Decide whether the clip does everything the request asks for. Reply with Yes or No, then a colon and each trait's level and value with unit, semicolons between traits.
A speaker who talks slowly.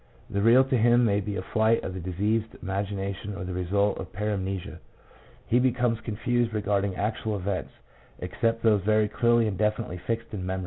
No: average, 180 wpm